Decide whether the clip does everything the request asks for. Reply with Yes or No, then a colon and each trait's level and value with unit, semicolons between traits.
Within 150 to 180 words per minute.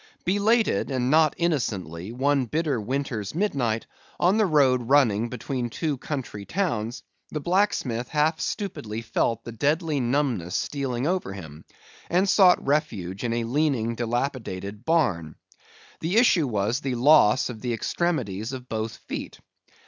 No: average, 140 wpm